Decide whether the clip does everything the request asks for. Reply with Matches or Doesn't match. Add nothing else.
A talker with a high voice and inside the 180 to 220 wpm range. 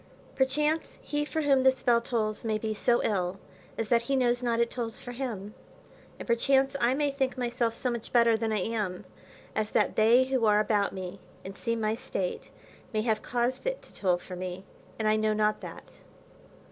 Matches